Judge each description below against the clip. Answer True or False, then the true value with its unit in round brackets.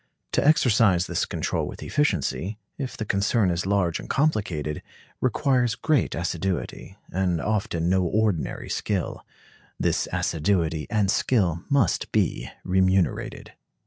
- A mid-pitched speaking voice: False (95 Hz)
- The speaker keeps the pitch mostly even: False (4.4 semitones)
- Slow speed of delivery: True (120 wpm)